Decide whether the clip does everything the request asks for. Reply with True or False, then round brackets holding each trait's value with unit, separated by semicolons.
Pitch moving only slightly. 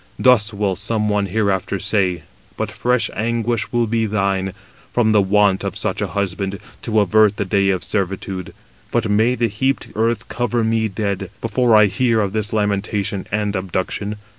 True (2.3 semitones)